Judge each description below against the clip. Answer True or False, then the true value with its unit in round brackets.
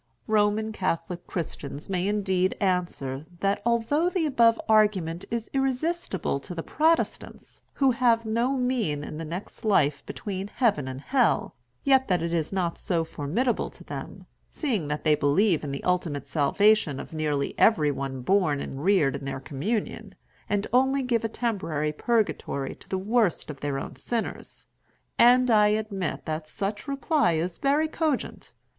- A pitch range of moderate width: False (7.2 semitones)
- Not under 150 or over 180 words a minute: True (160 wpm)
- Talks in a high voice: True (195 Hz)